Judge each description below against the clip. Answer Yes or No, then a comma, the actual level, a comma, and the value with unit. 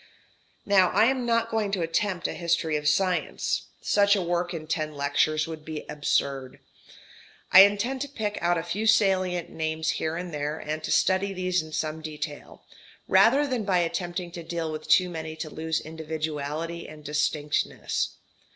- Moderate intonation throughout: Yes, average, 3.6 semitones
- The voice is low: No, medium, 170 Hz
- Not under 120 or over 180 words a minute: Yes, average, 170 wpm